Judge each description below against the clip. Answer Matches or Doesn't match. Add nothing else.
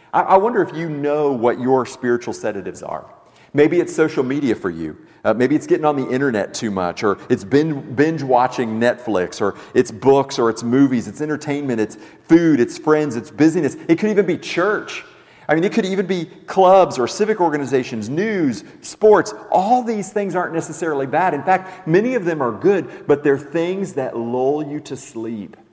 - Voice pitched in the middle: Matches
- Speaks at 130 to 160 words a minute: Doesn't match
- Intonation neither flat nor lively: Doesn't match